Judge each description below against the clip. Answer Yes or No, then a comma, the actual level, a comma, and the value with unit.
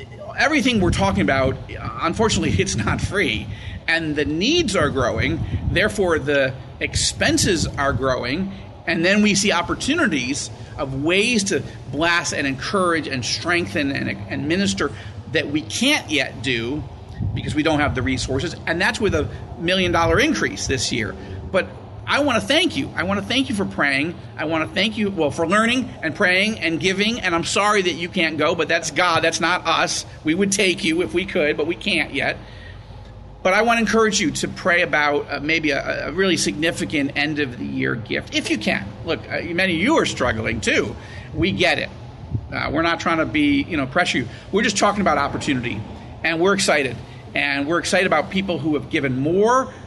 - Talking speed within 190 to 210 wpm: Yes, average, 195 wpm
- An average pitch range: No, wide, 6.9 semitones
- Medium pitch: Yes, medium, 160 Hz